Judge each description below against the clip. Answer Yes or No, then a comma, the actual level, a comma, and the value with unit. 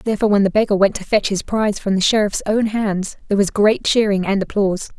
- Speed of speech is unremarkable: No, fast, 240 wpm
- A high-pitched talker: Yes, high, 205 Hz